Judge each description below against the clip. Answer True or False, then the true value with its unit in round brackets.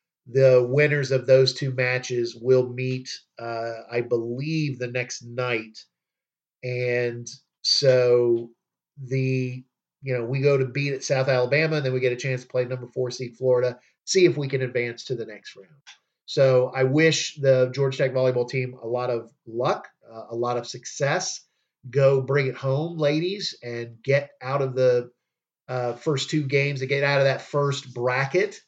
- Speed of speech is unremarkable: True (180 wpm)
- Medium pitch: False (130 Hz)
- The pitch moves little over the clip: True (2.1 semitones)